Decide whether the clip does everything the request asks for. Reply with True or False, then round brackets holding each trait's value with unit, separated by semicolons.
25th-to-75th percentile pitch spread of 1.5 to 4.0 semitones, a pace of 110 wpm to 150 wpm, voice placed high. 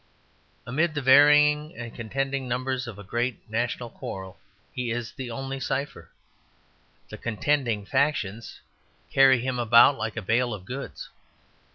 False (2.9 semitones; 140 wpm; 125 Hz)